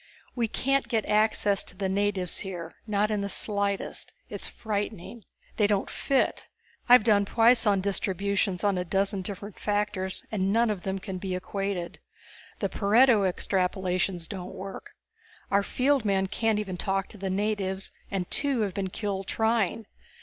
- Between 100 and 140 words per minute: No, average, 155 wpm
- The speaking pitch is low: No, high, 200 Hz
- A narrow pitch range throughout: Yes, narrow, 2.0 semitones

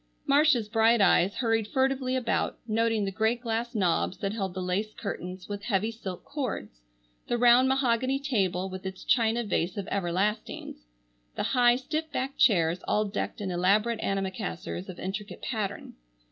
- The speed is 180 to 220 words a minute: No, average, 160 wpm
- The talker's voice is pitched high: Yes, high, 215 Hz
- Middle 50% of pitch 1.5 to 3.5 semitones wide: No, average, 4.2 semitones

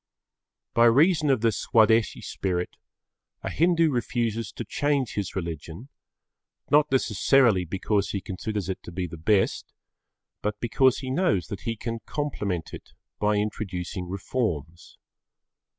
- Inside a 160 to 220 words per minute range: No, slow, 135 wpm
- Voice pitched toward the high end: No, low, 110 Hz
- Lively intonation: Yes, wide, 5.7 semitones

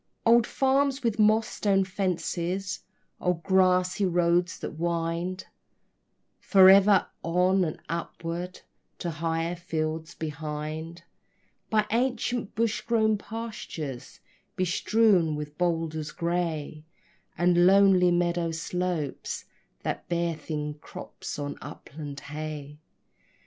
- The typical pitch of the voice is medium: Yes, medium, 175 Hz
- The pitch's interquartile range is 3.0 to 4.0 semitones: Yes, average, 3.4 semitones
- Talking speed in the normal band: No, slow, 100 wpm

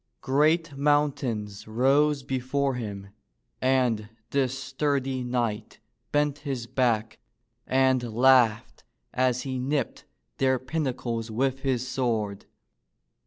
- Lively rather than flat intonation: No, average, 2.7 semitones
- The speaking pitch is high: No, low, 130 Hz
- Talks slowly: Yes, slow, 100 wpm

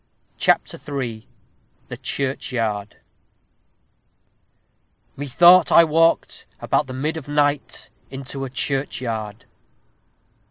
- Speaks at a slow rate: Yes, slow, 90 wpm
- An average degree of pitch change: Yes, average, 3.3 semitones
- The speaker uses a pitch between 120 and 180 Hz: Yes, low, 135 Hz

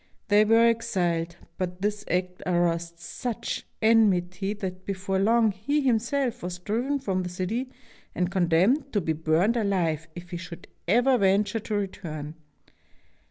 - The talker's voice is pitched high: Yes, high, 195 Hz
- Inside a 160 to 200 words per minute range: No, average, 145 wpm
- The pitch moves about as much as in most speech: Yes, average, 4.2 semitones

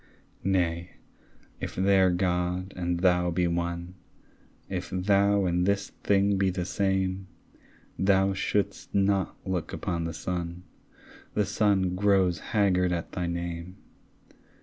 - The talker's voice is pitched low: Yes, very low, 90 Hz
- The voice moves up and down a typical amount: No, narrow, 1.8 semitones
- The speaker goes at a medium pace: No, slow, 125 wpm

